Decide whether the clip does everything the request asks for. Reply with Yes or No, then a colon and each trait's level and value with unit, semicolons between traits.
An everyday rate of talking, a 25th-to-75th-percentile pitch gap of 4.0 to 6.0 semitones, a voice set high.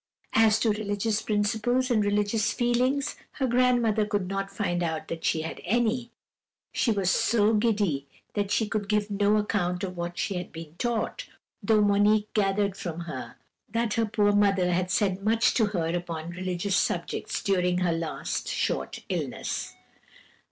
No: average, 160 wpm; average, 3.4 semitones; high, 205 Hz